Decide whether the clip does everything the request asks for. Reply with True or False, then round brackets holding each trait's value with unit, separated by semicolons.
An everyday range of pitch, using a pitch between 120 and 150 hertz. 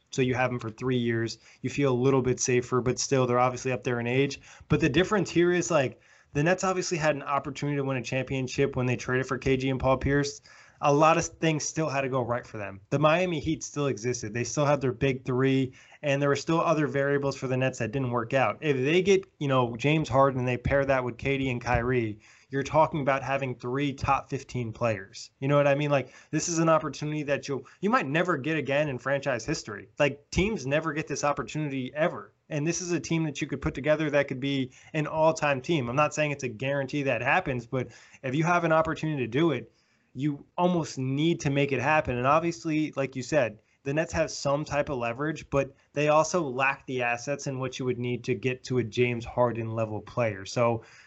True (3.3 semitones; 140 Hz)